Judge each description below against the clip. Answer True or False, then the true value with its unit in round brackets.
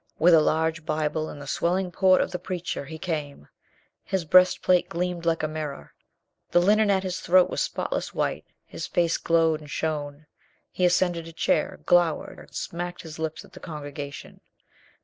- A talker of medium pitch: True (165 Hz)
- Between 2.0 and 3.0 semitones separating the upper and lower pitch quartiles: True (2.5 semitones)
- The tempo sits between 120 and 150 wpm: False (175 wpm)